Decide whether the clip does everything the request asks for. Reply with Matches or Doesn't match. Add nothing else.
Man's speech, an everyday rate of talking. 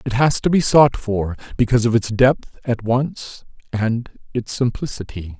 Matches